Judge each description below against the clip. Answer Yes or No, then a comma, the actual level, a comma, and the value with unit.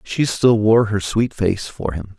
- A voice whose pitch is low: Yes, low, 105 Hz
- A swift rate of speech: Yes, fast, 220 wpm